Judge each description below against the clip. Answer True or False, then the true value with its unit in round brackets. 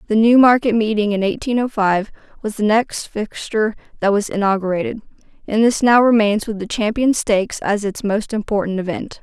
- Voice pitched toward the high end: True (215 Hz)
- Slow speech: False (175 wpm)